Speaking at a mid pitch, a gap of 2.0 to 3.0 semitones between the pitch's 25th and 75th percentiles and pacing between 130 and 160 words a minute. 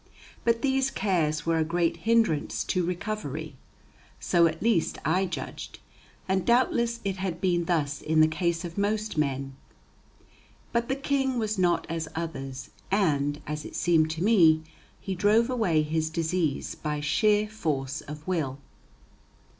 No: medium, 170 Hz; average, 5.2 semitones; average, 150 wpm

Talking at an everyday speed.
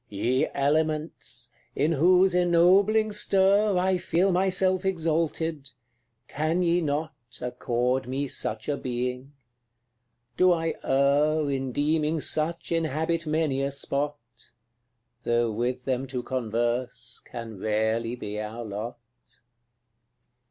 No: slow, 110 wpm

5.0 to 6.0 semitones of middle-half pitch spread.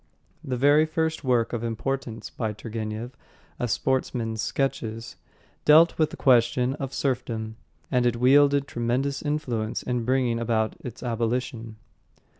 No: average, 3.0 semitones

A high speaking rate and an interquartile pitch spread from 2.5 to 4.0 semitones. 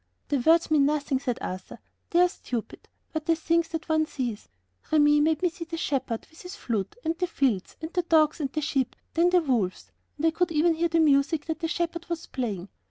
Yes: fast, 225 wpm; average, 3.5 semitones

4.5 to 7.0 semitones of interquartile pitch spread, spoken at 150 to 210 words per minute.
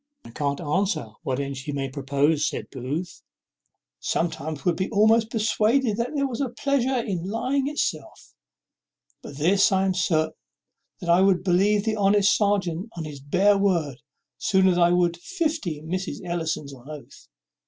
Yes: wide, 5.5 semitones; average, 165 wpm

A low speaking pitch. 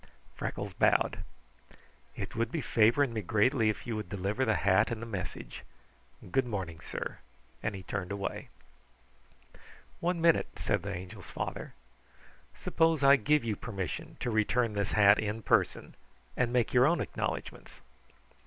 Yes: low, 110 Hz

